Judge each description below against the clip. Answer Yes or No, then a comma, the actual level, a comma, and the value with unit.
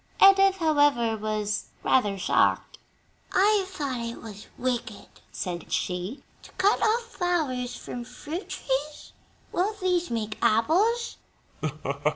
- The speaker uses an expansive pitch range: Yes, wide, 8.7 semitones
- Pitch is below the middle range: No, very high, 270 Hz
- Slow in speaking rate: Yes, slow, 115 wpm